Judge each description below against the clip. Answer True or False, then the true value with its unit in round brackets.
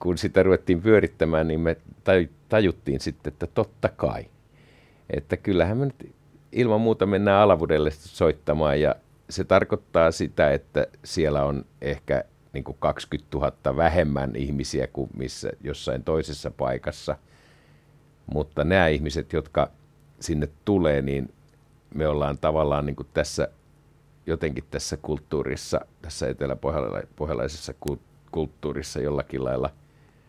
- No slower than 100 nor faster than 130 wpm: True (110 wpm)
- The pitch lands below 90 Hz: True (80 Hz)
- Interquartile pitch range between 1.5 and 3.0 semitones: False (4.1 semitones)